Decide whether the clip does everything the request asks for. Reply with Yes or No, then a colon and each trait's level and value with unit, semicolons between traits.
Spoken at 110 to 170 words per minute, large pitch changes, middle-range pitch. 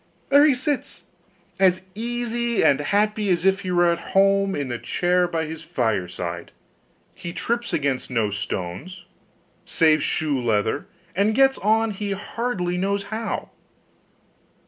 Yes: average, 140 wpm; wide, 6.6 semitones; medium, 180 Hz